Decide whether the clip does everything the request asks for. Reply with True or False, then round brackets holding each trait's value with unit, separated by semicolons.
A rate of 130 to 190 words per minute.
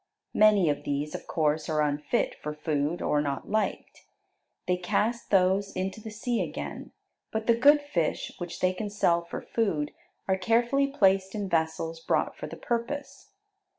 True (165 wpm)